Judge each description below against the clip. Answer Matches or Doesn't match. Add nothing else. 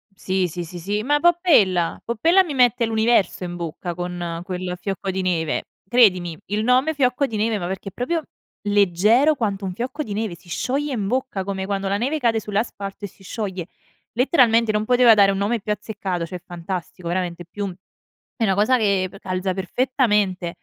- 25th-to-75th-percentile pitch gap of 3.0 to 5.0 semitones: Matches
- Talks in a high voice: Matches